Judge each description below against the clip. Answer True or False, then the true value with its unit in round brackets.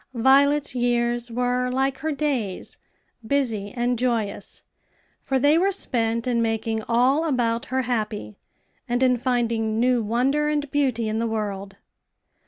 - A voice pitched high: True (245 Hz)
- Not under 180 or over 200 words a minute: False (140 wpm)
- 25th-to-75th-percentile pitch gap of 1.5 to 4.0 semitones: True (2.8 semitones)